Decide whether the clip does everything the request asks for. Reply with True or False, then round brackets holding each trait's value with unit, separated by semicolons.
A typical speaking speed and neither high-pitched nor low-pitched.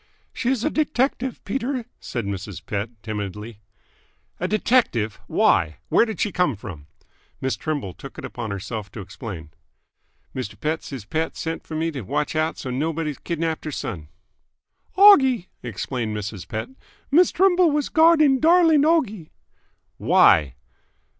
True (145 wpm; 155 Hz)